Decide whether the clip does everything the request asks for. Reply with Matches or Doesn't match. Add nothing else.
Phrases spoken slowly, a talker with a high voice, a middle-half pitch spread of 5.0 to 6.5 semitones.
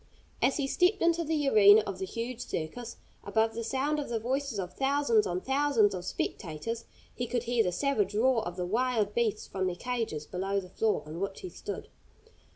Doesn't match